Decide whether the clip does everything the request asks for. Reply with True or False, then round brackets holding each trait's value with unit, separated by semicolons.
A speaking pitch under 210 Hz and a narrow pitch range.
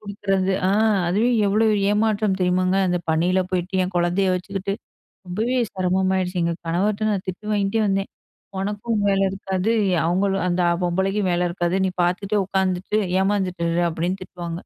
True (190 Hz; 2.0 semitones)